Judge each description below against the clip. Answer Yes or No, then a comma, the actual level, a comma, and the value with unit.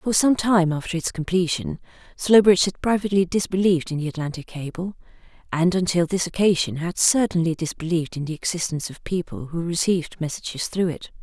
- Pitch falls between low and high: Yes, medium, 175 Hz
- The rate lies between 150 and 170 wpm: Yes, average, 165 wpm